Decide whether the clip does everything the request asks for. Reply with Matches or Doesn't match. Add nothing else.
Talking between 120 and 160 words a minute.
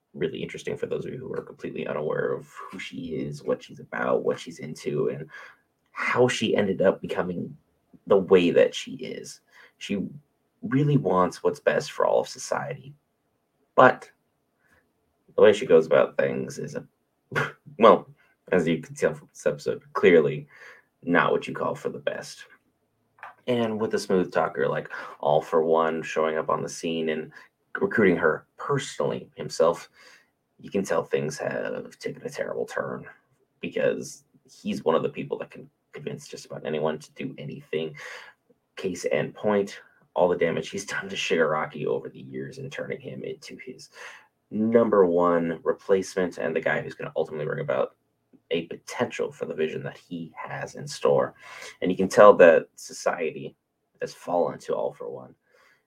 Doesn't match